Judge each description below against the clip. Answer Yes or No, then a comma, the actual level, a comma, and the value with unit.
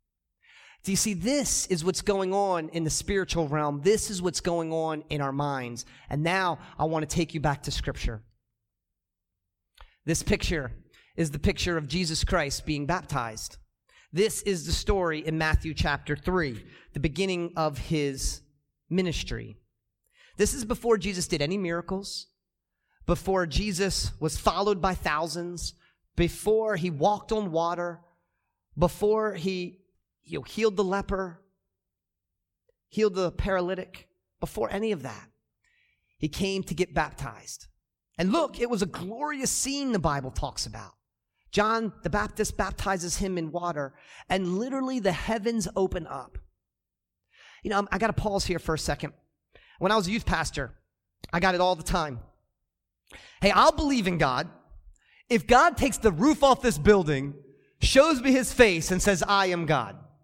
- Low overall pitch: No, medium, 180 Hz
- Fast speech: No, average, 155 wpm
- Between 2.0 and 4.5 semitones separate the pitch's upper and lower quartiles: No, average, 5.2 semitones